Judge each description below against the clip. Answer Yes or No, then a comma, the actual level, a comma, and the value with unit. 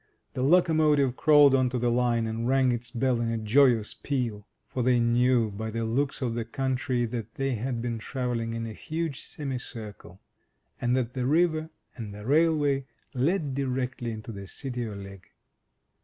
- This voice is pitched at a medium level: No, low, 125 Hz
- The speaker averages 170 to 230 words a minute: Yes, average, 180 wpm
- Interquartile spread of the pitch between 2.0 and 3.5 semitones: Yes, average, 2.9 semitones